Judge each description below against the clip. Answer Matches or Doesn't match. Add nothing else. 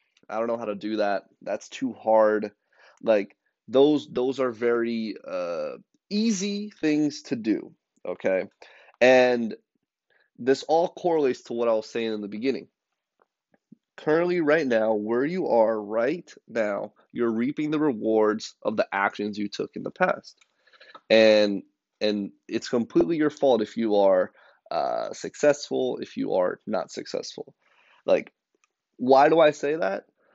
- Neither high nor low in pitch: Doesn't match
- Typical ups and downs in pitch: Doesn't match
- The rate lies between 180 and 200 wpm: Doesn't match